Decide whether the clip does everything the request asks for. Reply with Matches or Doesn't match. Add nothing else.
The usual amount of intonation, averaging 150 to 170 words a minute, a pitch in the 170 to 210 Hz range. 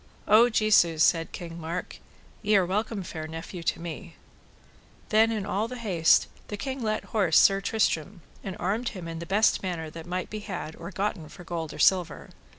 Doesn't match